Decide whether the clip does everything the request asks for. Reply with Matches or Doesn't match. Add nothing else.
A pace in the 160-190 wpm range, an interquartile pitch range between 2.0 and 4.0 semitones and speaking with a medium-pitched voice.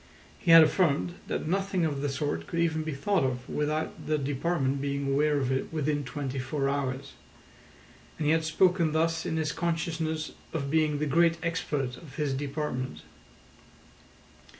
Matches